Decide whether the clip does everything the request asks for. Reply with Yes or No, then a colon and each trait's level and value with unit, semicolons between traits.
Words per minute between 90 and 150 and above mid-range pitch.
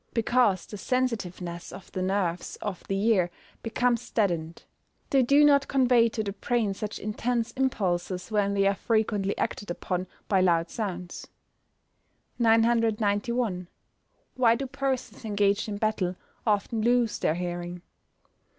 Yes: slow, 135 wpm; high, 210 Hz